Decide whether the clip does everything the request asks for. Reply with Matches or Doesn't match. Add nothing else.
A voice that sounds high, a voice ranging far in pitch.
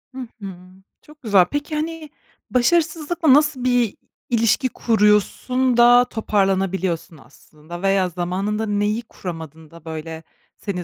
Matches